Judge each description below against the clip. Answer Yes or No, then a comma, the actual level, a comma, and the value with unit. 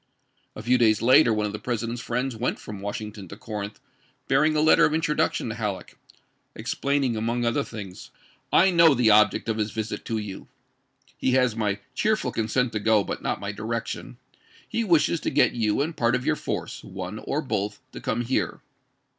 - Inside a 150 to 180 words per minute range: No, average, 200 wpm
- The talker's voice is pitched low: Yes, low, 115 Hz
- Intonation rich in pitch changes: No, average, 3.6 semitones